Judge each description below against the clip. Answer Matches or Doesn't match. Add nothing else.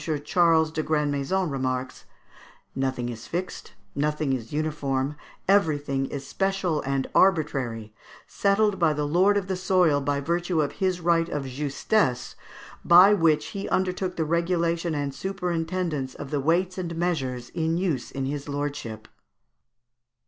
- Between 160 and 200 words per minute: Doesn't match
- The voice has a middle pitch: Matches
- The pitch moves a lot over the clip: Doesn't match